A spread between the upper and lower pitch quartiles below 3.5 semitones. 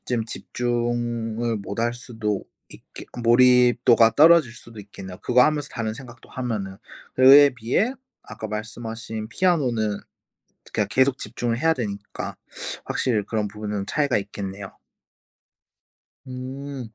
Yes: average, 2.9 semitones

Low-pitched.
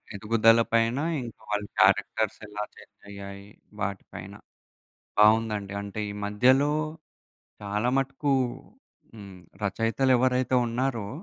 Yes: low, 110 Hz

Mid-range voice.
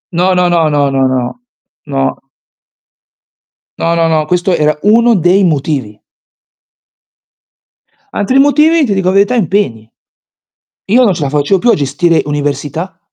Yes: medium, 170 Hz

